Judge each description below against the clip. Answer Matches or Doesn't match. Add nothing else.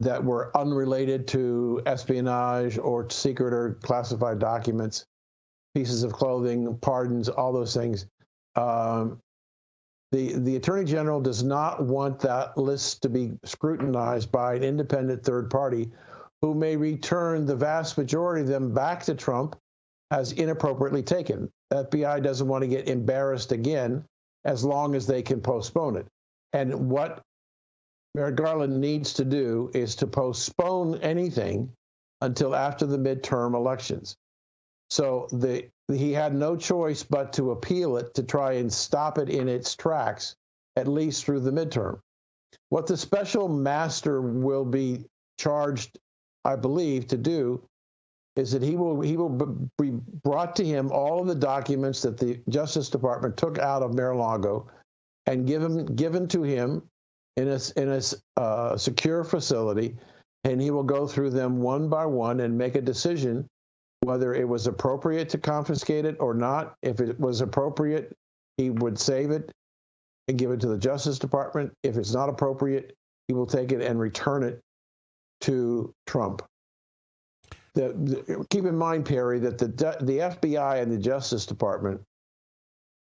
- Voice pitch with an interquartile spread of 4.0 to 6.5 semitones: Doesn't match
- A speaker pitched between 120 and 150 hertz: Matches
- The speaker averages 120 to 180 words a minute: Matches